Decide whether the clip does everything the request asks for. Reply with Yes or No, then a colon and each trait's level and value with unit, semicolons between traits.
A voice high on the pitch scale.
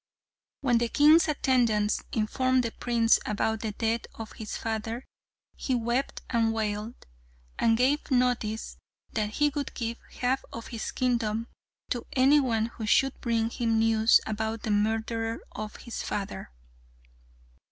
Yes: high, 230 Hz